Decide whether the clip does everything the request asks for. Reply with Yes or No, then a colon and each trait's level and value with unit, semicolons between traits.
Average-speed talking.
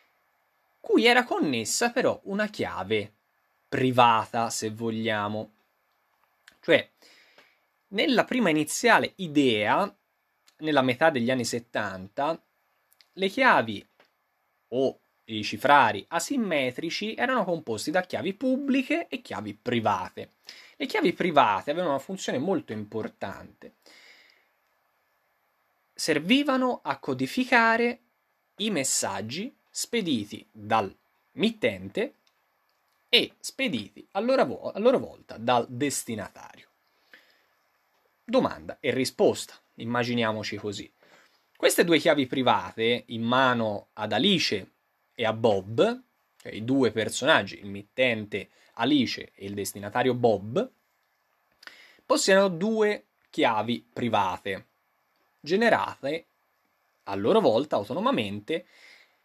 No: slow, 95 wpm